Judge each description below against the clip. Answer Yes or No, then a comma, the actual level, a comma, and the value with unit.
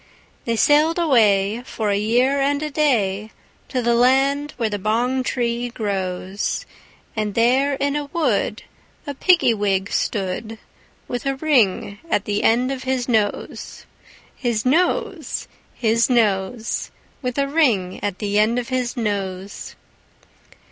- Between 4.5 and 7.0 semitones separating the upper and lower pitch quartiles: Yes, average, 4.8 semitones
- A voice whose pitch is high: Yes, high, 235 Hz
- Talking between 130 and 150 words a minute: Yes, average, 140 wpm